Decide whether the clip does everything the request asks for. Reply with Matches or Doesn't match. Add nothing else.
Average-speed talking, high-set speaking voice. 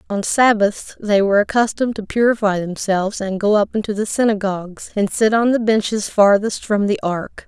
Matches